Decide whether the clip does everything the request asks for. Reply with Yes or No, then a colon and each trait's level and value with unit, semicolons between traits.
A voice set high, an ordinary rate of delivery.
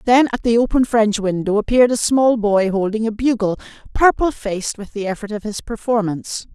Yes: high, 220 Hz; average, 195 wpm